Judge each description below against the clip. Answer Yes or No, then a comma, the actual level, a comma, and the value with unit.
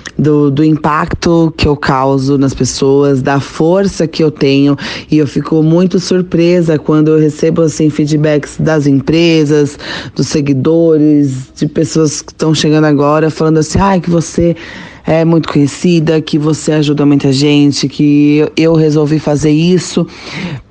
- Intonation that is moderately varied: No, narrow, 1.9 semitones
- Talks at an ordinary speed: Yes, average, 150 wpm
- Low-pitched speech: No, medium, 155 Hz